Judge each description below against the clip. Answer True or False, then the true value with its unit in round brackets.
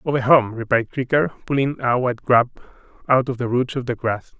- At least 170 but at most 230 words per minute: True (205 wpm)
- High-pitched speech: False (125 Hz)